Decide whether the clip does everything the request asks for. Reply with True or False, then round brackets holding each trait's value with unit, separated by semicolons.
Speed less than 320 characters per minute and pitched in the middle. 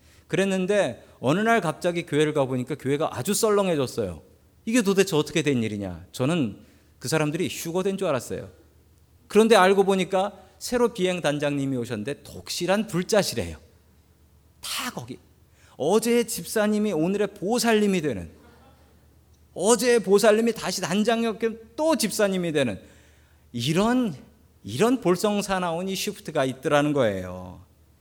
True (305 characters per minute; 165 Hz)